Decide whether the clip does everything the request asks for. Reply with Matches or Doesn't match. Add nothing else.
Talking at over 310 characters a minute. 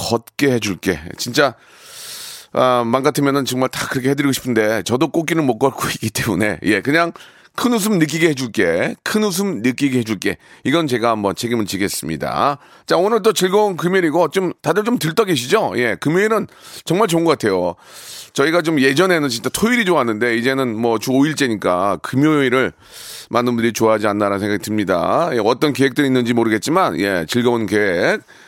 Matches